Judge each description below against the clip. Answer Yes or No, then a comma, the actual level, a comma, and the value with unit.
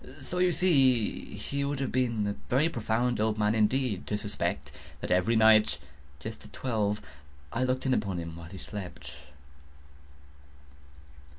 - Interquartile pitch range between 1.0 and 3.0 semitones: No, average, 4.0 semitones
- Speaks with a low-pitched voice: Yes, low, 110 Hz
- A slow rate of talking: No, average, 155 wpm